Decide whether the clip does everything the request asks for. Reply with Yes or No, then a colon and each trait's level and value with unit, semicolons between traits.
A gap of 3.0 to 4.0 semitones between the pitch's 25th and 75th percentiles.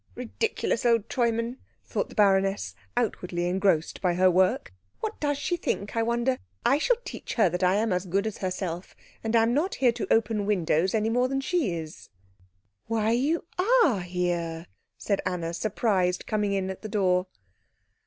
No: average, 4.7 semitones